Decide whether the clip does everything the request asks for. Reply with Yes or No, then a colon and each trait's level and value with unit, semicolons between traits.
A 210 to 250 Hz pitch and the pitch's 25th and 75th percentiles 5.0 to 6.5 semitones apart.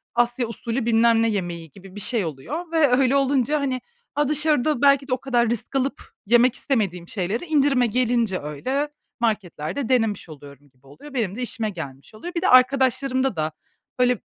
Yes: high, 240 Hz; wide, 5.6 semitones